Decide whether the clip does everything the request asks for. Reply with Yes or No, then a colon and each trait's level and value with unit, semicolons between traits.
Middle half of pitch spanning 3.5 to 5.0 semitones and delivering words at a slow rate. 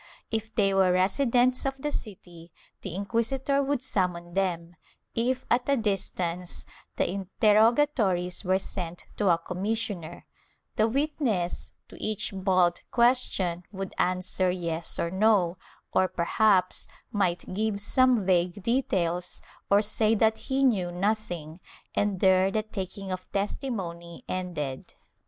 Yes: average, 3.8 semitones; slow, 130 wpm